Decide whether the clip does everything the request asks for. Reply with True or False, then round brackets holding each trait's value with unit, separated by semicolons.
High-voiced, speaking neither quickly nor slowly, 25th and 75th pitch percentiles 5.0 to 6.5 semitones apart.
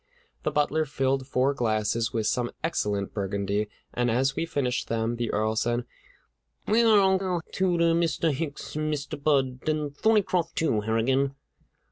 False (135 Hz; 150 wpm; 5.4 semitones)